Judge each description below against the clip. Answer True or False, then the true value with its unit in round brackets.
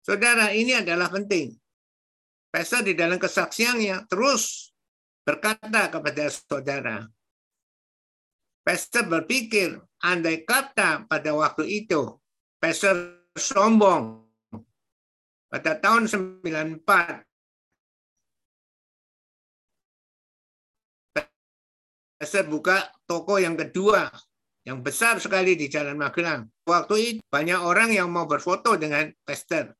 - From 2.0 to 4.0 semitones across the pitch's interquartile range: False (5.5 semitones)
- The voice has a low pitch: False (175 Hz)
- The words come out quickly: False (90 wpm)